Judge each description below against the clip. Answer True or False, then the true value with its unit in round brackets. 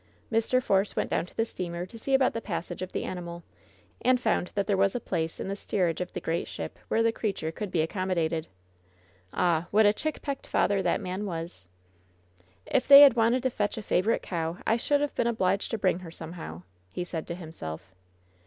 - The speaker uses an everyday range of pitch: True (4.8 semitones)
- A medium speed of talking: False (210 wpm)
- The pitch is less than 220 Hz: True (185 Hz)